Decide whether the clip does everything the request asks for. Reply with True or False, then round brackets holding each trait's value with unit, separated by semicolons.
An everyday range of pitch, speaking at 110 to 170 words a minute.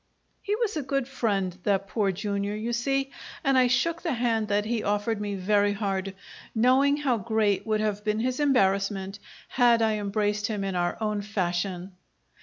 False (3.6 semitones; 180 wpm)